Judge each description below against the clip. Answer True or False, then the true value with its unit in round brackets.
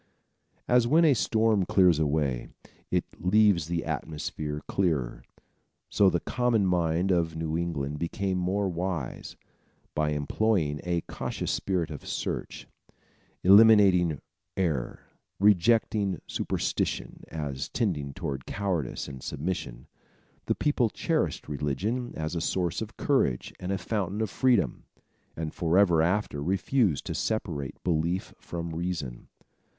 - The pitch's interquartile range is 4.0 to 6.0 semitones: True (4.7 semitones)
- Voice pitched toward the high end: False (85 Hz)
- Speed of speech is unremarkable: False (125 wpm)